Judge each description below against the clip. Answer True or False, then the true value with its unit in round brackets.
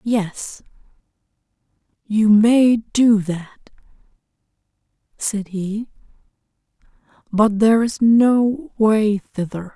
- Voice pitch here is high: True (215 Hz)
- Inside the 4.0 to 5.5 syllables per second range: False (2.8 syllables/s)